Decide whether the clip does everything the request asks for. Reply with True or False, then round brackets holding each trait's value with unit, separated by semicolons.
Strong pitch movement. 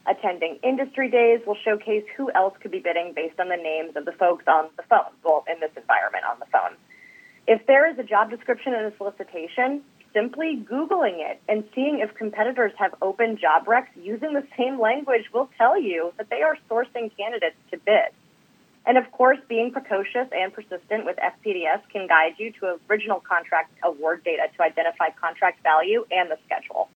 True (6.0 semitones)